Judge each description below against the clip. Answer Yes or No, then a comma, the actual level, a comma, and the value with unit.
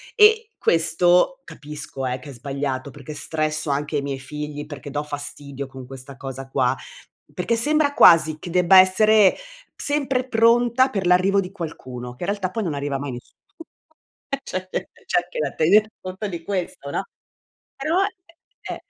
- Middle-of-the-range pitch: Yes, medium, 165 Hz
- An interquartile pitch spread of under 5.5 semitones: No, wide, 6.4 semitones